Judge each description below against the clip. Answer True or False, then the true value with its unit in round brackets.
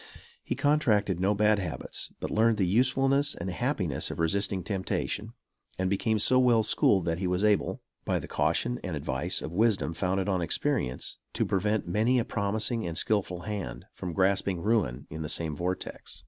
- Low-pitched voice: True (100 Hz)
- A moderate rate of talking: True (175 wpm)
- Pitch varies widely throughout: False (3.8 semitones)